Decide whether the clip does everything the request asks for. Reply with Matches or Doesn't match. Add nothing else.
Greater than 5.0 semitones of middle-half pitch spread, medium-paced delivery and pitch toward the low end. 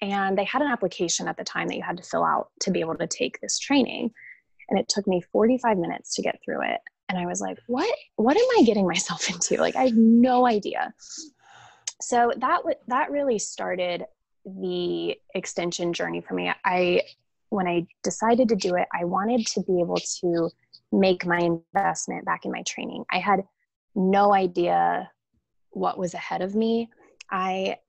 Doesn't match